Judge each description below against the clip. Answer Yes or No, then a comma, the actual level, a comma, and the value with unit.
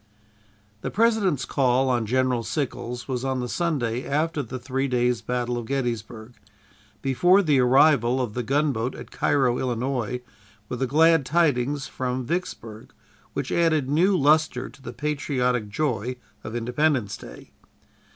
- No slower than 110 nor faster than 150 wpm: Yes, average, 140 wpm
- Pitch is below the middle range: Yes, low, 130 Hz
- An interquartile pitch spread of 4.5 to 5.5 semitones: No, average, 3.3 semitones